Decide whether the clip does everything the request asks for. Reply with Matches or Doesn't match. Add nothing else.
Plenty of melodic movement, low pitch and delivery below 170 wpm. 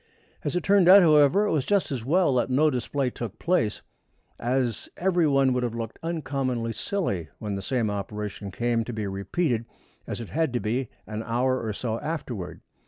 Doesn't match